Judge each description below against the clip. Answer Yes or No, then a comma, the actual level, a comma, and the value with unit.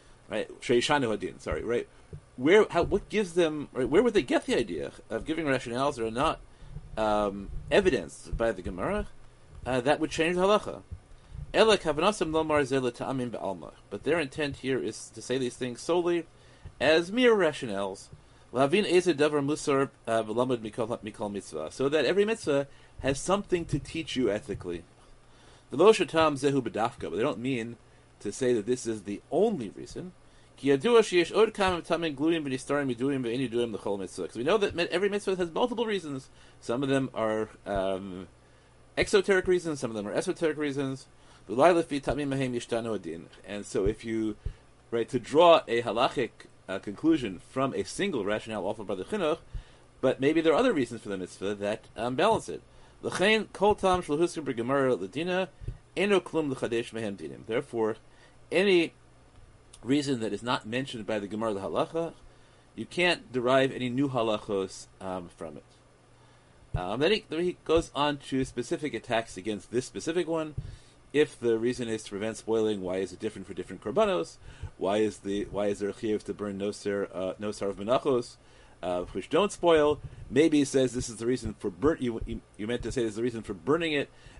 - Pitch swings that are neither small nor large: No, wide, 6.4 semitones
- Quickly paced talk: No, average, 150 wpm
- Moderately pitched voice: No, low, 130 Hz